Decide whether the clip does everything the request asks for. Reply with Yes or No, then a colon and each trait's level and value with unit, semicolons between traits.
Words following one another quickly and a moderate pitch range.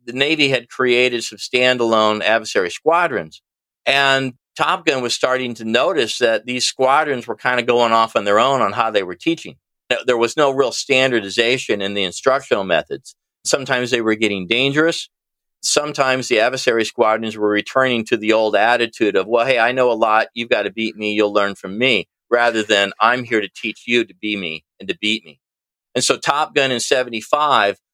No: average, 195 wpm; average, 3.1 semitones